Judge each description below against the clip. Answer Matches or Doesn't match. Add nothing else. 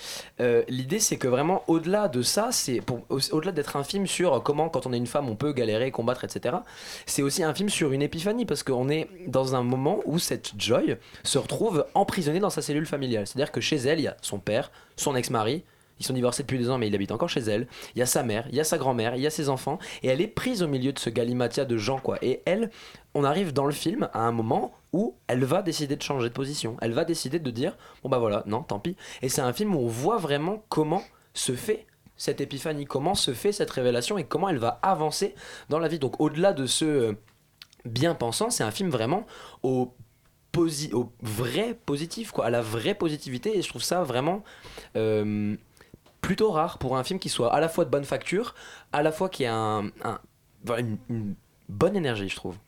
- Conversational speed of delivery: Doesn't match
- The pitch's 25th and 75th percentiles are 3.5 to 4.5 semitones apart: Doesn't match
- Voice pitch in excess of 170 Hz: Doesn't match